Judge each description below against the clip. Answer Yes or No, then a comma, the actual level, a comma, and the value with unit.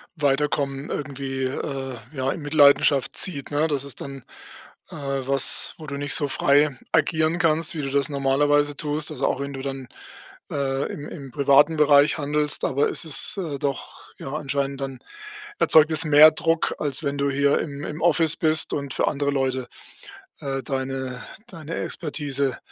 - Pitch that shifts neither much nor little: No, narrow, 1.8 semitones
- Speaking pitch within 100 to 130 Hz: No, medium, 140 Hz